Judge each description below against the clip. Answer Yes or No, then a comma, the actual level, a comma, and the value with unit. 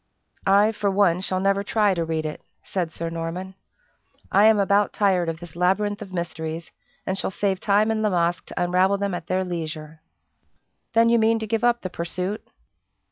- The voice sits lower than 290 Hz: Yes, high, 190 Hz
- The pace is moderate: Yes, average, 190 wpm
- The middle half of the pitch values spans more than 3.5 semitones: No, average, 3.2 semitones